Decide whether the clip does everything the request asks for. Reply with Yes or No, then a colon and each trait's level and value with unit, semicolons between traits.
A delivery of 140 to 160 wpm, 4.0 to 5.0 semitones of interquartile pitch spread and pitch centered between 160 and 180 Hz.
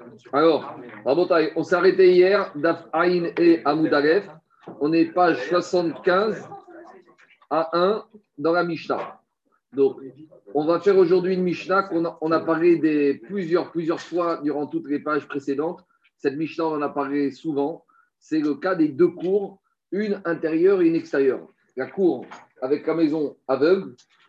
Yes: average, 150 wpm; average, 4.5 semitones; medium, 170 Hz